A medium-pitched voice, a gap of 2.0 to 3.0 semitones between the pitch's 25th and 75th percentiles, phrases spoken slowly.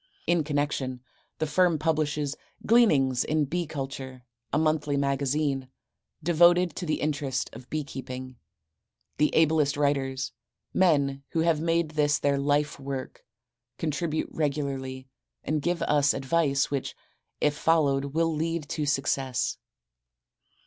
Yes: medium, 145 Hz; narrow, 2.5 semitones; slow, 125 wpm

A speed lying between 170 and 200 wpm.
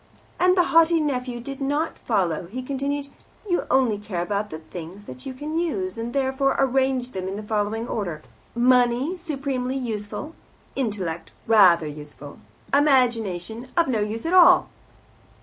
No: average, 150 wpm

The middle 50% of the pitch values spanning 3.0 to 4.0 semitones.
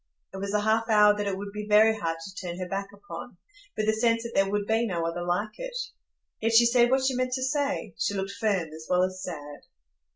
Yes: average, 3.4 semitones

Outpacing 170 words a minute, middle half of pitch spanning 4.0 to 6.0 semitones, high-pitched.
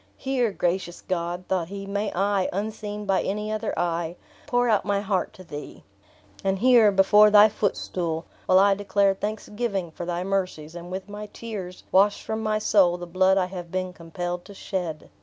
No: average, 180 wpm; average, 2.7 semitones; high, 195 Hz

